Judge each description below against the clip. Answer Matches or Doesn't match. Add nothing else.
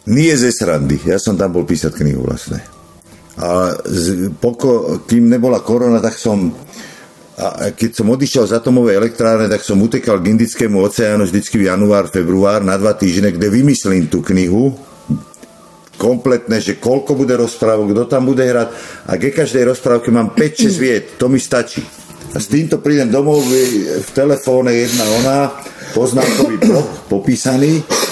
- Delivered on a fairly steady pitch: Doesn't match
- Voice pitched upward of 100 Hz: Matches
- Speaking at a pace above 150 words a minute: Matches